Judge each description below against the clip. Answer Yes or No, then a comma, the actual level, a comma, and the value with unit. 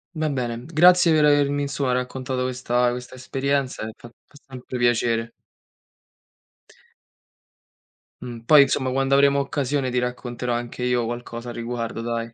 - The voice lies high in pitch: No, low, 125 Hz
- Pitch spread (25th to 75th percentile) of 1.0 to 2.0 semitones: No, narrow, 2.5 semitones